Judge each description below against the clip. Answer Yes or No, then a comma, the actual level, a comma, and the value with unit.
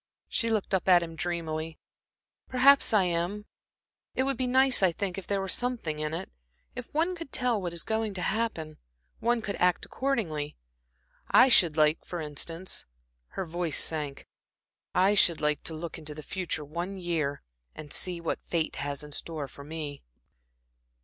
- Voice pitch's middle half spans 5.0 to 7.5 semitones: Yes, wide, 5.5 semitones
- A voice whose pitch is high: No, medium, 175 Hz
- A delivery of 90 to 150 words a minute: No, average, 175 wpm